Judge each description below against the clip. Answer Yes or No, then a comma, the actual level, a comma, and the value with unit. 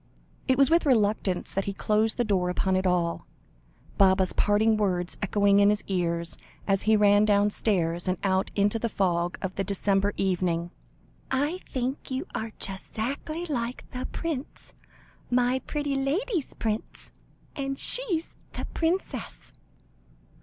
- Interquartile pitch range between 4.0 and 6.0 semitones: Yes, wide, 5.6 semitones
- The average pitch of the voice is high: Yes, high, 210 Hz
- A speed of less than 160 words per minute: Yes, average, 145 wpm